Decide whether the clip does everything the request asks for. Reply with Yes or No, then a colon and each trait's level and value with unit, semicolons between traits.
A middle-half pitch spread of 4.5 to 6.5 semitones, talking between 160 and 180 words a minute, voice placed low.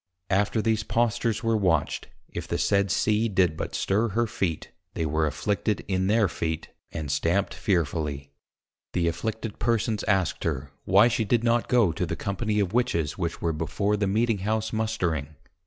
Yes: average, 4.9 semitones; average, 170 wpm; low, 100 Hz